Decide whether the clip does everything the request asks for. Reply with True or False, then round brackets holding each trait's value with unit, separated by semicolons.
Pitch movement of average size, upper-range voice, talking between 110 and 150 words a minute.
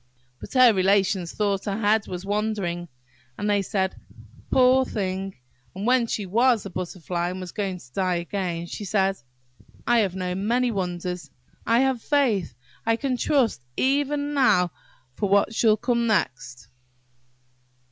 True (4.3 semitones; 200 Hz; 145 wpm)